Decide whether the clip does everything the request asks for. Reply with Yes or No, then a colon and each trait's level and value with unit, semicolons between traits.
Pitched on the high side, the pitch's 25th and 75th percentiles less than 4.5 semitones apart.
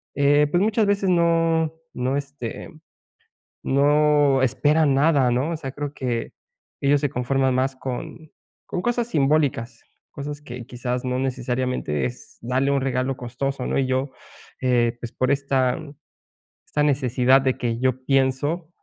No: low, 135 Hz; narrow, 2.5 semitones